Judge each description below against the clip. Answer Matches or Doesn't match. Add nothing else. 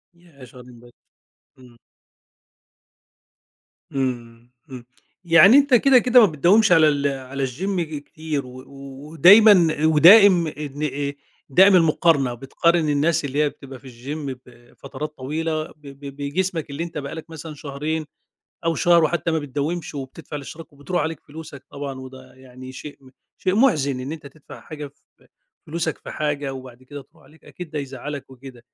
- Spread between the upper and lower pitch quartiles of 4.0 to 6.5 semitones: Doesn't match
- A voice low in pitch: Doesn't match